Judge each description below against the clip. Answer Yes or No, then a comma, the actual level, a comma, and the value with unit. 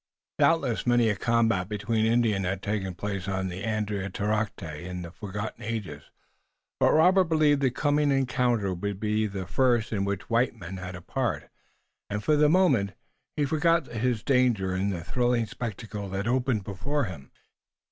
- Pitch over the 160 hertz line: No, low, 110 Hz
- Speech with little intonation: No, average, 4.4 semitones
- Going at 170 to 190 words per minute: No, average, 160 wpm